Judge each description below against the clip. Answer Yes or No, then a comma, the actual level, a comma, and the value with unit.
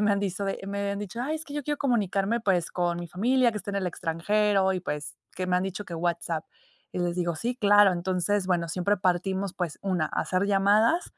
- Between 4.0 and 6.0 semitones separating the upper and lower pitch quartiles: No, average, 2.7 semitones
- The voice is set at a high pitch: Yes, high, 195 Hz